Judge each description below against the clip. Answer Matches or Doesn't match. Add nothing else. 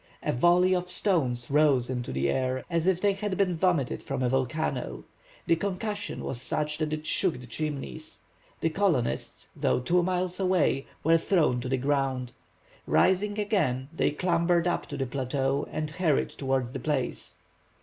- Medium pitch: Matches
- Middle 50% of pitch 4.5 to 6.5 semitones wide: Matches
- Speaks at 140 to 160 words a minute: Doesn't match